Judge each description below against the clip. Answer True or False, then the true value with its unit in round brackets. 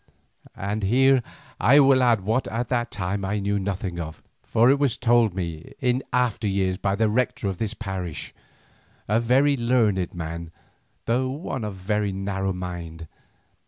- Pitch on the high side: False (105 Hz)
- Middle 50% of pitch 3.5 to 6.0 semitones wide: True (4.4 semitones)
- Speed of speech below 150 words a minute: False (160 wpm)